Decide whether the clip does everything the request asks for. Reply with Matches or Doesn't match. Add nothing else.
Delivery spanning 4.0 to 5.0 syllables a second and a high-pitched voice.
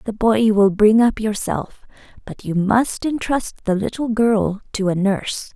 Matches